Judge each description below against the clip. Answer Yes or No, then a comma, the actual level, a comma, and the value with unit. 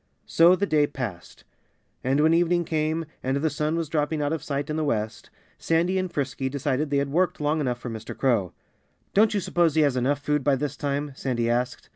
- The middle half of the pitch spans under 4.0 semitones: Yes, average, 3.3 semitones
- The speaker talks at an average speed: No, fast, 215 wpm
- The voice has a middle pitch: Yes, medium, 145 Hz